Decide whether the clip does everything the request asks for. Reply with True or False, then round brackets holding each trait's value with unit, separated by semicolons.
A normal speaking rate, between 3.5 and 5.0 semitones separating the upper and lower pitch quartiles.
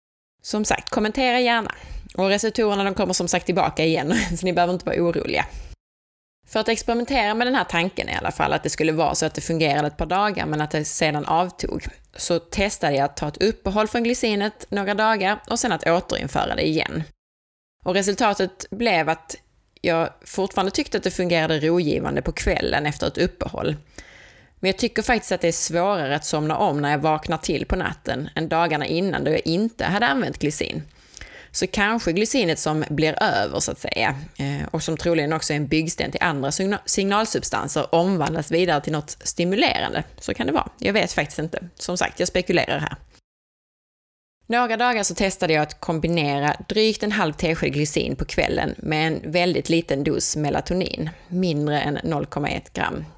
True (185 wpm; 4.7 semitones)